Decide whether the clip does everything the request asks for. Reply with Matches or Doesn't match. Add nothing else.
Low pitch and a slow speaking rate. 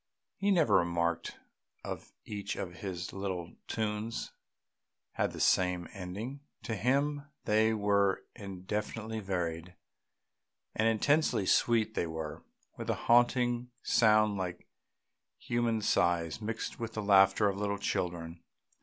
Matches